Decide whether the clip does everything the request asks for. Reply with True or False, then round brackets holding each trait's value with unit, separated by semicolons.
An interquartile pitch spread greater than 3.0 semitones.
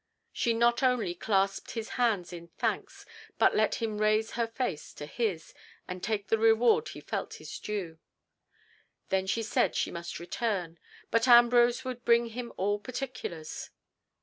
True (3.9 semitones)